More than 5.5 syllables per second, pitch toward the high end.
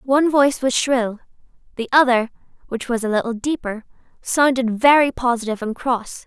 No: 5.3 syllables/s; high, 245 Hz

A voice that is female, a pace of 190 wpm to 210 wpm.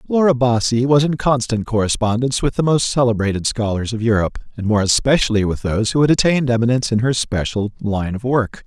No: male; average, 195 wpm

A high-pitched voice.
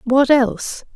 Yes: very high, 255 Hz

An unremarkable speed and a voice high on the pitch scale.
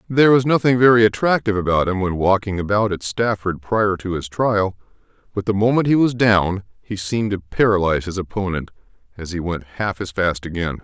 No: average, 195 wpm; low, 100 Hz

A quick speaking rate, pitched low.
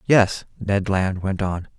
No: average, 170 wpm; low, 100 Hz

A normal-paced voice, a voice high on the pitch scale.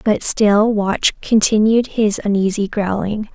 No: slow, 125 wpm; high, 210 Hz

